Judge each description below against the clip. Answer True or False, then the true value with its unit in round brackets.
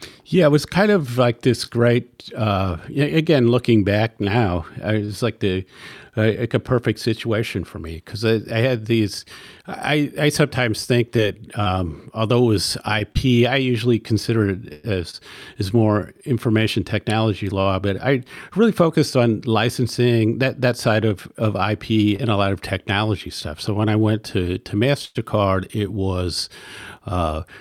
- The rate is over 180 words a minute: False (165 wpm)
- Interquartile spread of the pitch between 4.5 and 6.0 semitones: False (3.1 semitones)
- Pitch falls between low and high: False (110 Hz)